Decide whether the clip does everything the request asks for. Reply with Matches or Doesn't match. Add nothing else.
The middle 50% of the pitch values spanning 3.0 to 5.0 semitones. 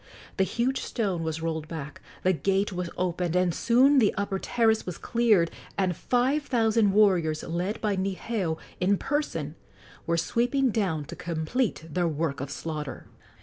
Doesn't match